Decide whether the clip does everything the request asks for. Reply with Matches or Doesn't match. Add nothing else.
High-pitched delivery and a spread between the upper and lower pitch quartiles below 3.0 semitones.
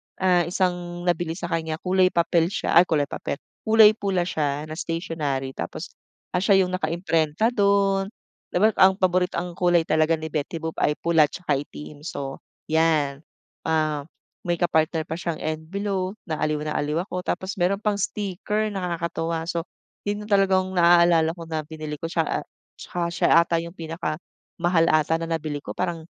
Doesn't match